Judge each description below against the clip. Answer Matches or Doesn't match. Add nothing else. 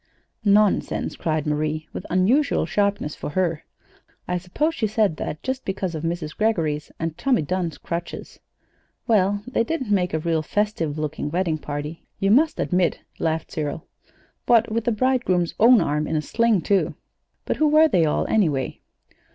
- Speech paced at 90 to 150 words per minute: Doesn't match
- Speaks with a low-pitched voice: Doesn't match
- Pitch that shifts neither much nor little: Doesn't match